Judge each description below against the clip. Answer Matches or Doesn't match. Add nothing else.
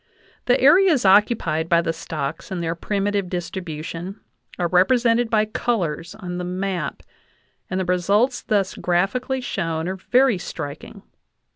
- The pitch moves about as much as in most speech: Matches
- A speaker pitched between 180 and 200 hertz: Matches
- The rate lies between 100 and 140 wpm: Matches